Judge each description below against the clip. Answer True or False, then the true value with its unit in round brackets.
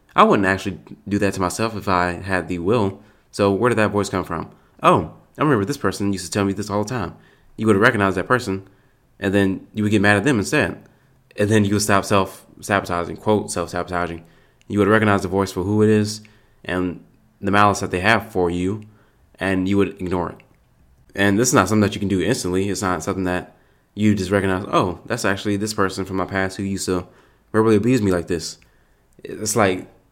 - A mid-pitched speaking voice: False (100 Hz)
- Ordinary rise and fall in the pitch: False (2.3 semitones)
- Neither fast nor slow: False (225 wpm)